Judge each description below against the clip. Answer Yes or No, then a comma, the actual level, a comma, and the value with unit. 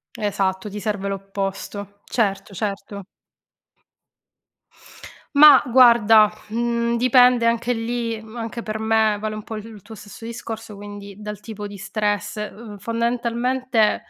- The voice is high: Yes, high, 220 Hz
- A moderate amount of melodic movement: No, narrow, 2.3 semitones